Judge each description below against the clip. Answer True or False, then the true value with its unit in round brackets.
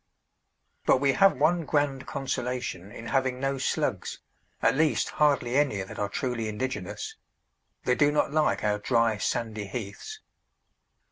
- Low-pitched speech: True (130 Hz)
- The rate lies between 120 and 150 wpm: True (140 wpm)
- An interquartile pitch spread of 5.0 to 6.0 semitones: False (4.5 semitones)